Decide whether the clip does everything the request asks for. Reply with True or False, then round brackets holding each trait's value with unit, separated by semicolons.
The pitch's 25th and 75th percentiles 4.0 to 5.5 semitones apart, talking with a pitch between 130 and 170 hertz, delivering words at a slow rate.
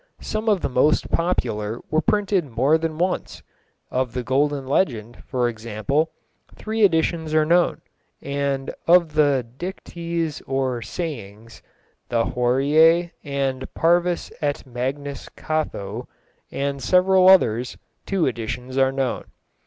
True (5.0 semitones; 140 Hz; 120 wpm)